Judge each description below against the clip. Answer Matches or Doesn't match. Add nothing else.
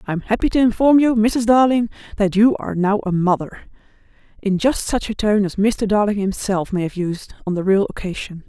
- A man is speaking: Doesn't match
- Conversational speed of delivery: Doesn't match